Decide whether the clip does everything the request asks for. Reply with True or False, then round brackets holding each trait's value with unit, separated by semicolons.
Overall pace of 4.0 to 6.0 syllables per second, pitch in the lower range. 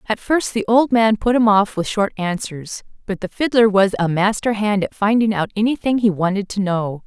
False (5.1 syllables/s; 210 Hz)